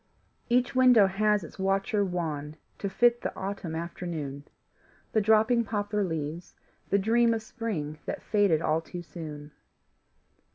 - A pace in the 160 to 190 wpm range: No, slow, 135 wpm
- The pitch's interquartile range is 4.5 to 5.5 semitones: Yes, average, 5.1 semitones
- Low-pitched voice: No, high, 195 Hz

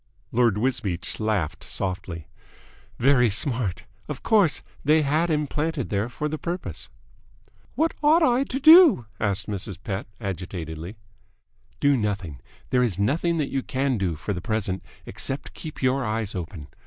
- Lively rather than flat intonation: Yes, wide, 7.5 semitones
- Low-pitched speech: Yes, low, 115 Hz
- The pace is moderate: Yes, average, 150 wpm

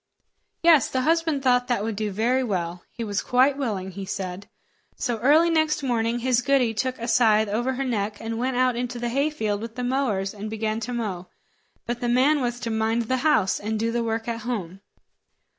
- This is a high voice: Yes, high, 235 Hz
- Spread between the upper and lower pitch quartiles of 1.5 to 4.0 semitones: Yes, average, 3.1 semitones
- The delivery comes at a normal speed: No, fast, 210 wpm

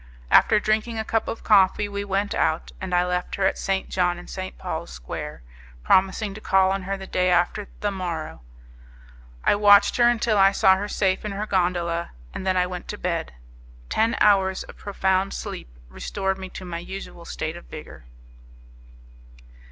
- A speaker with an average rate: Yes, average, 185 wpm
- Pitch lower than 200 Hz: Yes, high, 190 Hz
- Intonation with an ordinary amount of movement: No, narrow, 2.1 semitones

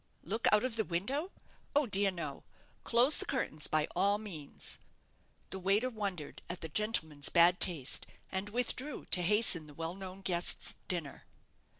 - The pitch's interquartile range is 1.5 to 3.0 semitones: No, average, 4.5 semitones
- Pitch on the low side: No, high, 190 Hz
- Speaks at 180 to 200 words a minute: No, average, 160 wpm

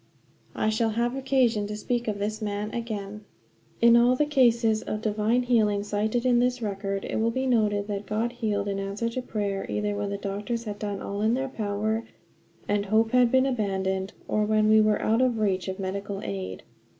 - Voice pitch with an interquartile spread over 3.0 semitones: No, narrow, 2.6 semitones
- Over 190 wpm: Yes, average, 200 wpm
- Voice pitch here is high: Yes, high, 215 Hz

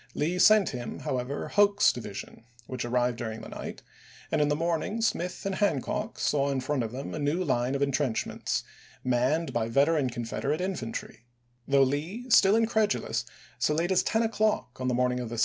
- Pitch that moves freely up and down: Yes, wide, 6.5 semitones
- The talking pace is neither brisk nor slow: Yes, average, 185 wpm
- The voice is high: No, medium, 140 Hz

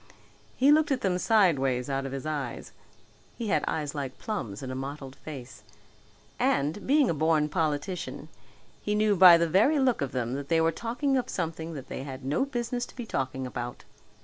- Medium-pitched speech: Yes, medium, 160 Hz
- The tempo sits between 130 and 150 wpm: No, average, 195 wpm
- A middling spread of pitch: No, wide, 8.0 semitones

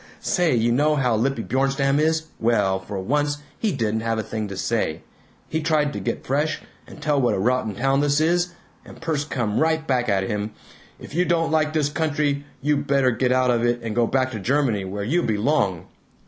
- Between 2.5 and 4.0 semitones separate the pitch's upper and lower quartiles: No, average, 5.0 semitones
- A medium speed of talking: No, fast, 210 wpm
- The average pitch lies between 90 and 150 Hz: Yes, low, 135 Hz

